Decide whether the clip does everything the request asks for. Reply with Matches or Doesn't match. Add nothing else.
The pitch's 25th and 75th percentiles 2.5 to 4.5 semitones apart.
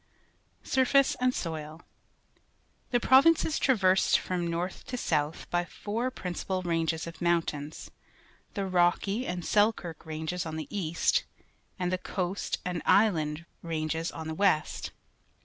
Matches